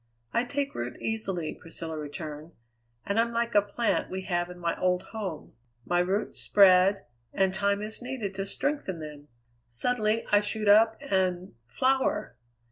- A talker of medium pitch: No, high, 195 Hz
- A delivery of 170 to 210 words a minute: No, average, 155 wpm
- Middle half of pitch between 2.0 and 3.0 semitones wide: No, average, 4.0 semitones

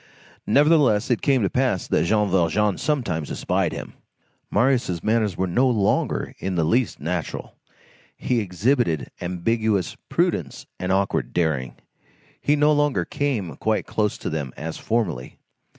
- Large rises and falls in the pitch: Yes, wide, 6.2 semitones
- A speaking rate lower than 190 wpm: Yes, average, 140 wpm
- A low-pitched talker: Yes, low, 105 Hz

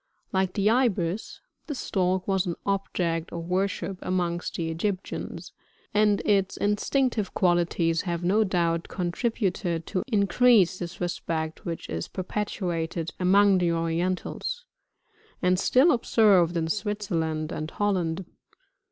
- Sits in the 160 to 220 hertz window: Yes, medium, 185 Hz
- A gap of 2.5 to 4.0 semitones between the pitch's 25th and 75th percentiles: Yes, average, 3.3 semitones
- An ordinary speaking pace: No, slow, 125 wpm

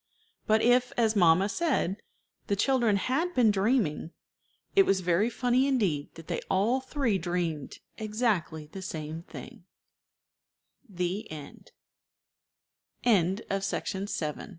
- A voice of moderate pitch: No, high, 200 Hz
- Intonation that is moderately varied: No, wide, 6.1 semitones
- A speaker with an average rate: No, slow, 105 wpm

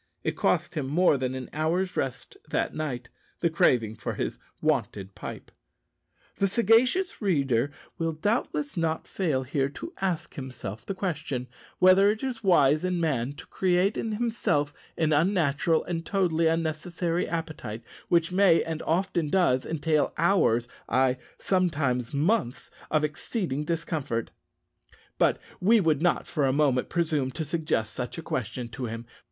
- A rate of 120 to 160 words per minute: Yes, average, 150 wpm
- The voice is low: No, medium, 160 Hz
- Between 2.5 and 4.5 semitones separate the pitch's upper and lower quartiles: No, average, 5.3 semitones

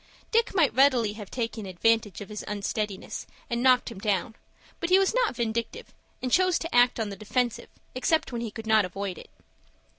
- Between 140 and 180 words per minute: No, average, 190 wpm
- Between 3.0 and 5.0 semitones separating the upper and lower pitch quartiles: Yes, average, 3.9 semitones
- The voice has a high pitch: Yes, high, 230 Hz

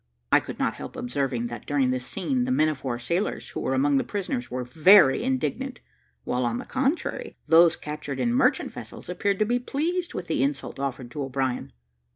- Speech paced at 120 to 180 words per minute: No, average, 200 wpm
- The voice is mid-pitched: Yes, medium, 155 Hz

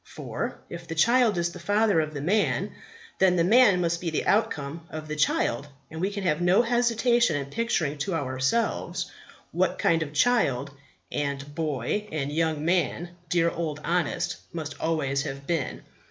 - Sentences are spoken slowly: No, average, 170 wpm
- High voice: No, medium, 165 Hz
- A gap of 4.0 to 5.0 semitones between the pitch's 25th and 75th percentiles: Yes, average, 4.7 semitones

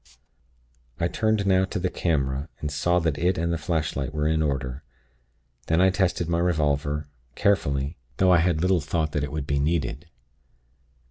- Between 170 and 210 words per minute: Yes, average, 175 wpm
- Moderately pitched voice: No, very low, 80 Hz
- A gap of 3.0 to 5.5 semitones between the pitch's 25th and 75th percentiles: Yes, average, 3.6 semitones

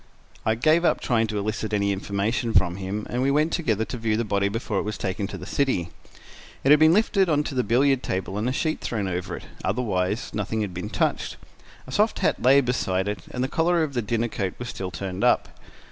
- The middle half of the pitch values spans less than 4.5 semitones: No, average, 5.1 semitones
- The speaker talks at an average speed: No, fast, 235 wpm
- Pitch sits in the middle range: No, low, 110 Hz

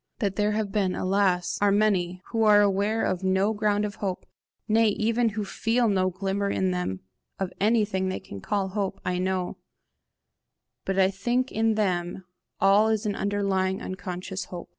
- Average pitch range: No, narrow, 2.1 semitones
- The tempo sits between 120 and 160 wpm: No, average, 170 wpm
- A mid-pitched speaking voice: No, high, 200 Hz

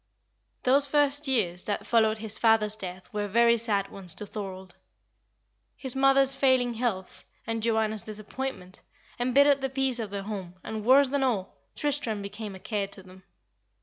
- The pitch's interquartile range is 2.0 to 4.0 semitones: No, average, 4.8 semitones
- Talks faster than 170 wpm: No, average, 165 wpm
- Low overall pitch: No, high, 220 Hz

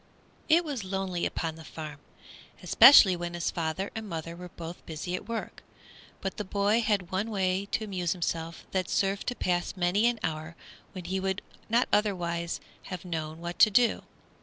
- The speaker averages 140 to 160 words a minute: No, average, 180 wpm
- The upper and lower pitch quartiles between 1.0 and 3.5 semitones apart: Yes, average, 3.2 semitones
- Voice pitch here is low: No, medium, 185 Hz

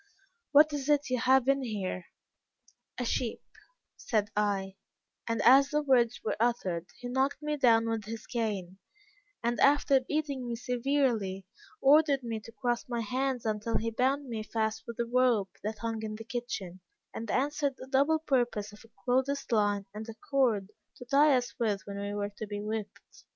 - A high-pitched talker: Yes, high, 235 Hz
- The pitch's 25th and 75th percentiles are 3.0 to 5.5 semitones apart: Yes, average, 3.8 semitones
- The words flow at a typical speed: Yes, average, 180 wpm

